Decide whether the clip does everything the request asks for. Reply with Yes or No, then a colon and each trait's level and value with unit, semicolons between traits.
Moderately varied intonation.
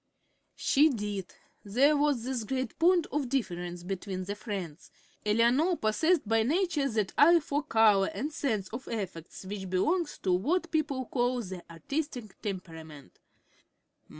No: wide, 7.1 semitones